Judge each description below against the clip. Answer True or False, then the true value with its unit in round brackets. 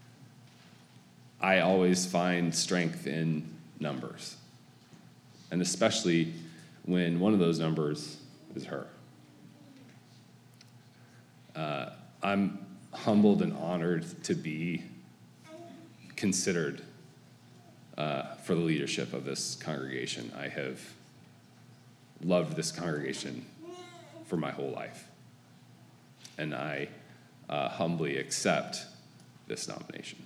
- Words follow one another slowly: True (90 wpm)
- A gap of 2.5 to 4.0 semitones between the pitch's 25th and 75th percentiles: True (3.4 semitones)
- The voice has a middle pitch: False (85 Hz)